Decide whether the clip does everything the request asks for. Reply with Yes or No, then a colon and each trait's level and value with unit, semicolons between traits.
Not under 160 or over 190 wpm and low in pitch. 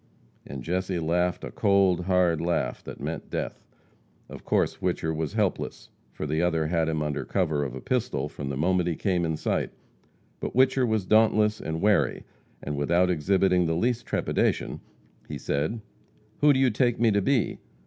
Yes: average, 180 wpm; very low, 90 Hz